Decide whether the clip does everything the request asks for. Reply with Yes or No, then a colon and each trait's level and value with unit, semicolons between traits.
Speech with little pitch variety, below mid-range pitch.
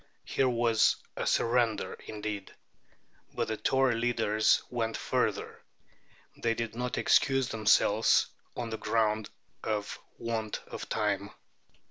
Yes: narrow, 1.9 semitones; low, 115 Hz